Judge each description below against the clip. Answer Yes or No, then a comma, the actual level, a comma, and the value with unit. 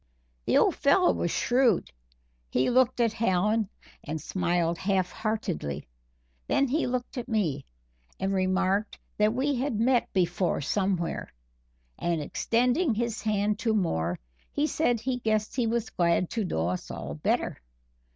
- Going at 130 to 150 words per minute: Yes, average, 145 wpm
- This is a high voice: Yes, high, 210 Hz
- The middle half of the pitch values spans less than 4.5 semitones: No, average, 5.3 semitones